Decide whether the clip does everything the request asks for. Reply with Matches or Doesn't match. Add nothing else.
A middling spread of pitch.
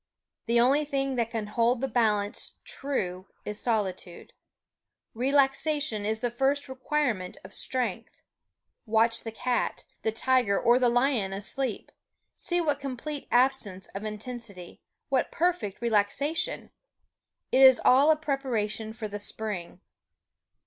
Matches